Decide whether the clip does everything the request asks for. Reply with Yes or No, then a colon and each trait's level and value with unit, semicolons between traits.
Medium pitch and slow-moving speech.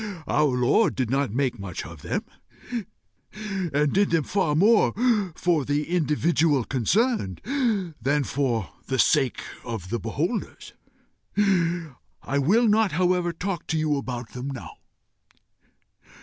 Yes: medium, 150 Hz; slow, 125 wpm